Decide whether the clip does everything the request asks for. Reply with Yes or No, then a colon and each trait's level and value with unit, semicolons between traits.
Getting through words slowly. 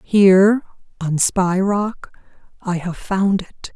Yes: slow, 130 wpm